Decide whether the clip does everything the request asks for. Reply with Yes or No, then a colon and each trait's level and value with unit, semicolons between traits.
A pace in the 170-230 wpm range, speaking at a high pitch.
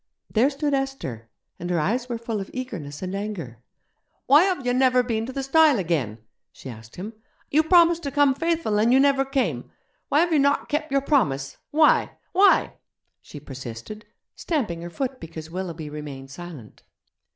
Yes: average, 175 wpm; high, 230 Hz